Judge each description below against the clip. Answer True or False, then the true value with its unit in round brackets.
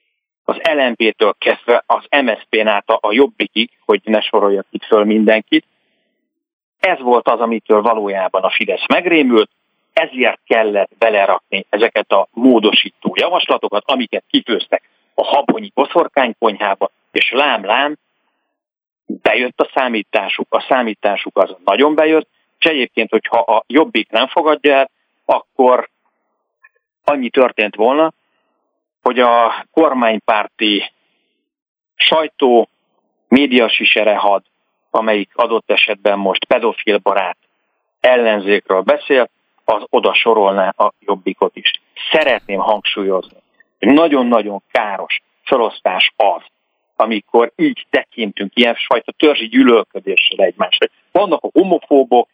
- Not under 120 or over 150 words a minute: False (105 wpm)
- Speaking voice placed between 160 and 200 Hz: False (135 Hz)